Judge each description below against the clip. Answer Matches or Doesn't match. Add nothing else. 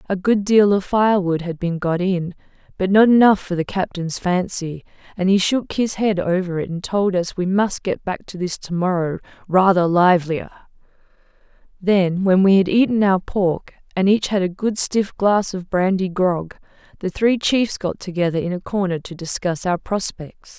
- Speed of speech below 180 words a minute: Doesn't match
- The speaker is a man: Doesn't match